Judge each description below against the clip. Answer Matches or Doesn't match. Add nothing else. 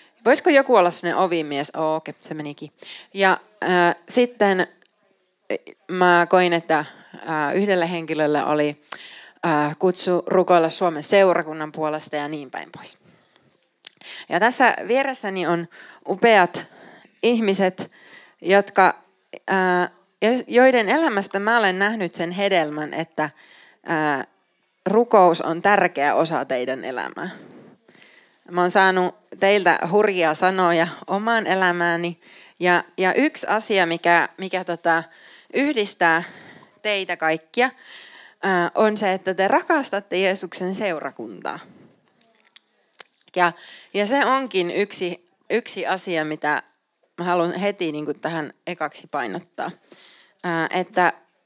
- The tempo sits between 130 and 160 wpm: Doesn't match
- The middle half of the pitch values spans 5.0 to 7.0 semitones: Doesn't match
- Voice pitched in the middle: Matches